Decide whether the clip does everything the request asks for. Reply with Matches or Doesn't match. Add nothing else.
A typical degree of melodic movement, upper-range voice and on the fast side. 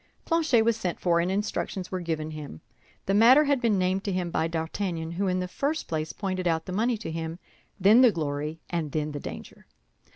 Doesn't match